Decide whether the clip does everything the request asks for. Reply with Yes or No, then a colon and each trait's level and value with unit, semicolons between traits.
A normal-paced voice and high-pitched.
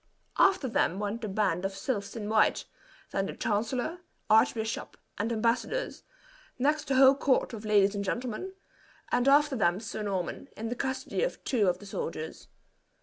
Yes: average, 165 wpm; high, 220 Hz